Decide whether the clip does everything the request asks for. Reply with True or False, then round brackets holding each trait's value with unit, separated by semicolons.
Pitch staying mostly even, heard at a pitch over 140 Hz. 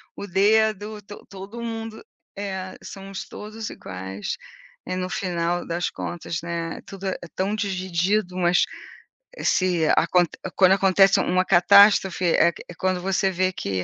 True (2.3 semitones; 185 Hz)